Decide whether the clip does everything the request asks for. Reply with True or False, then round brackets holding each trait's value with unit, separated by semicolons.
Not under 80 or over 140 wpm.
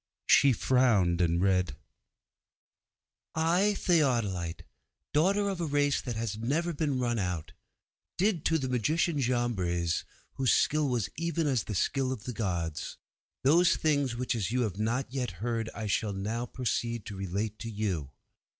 False (155 wpm)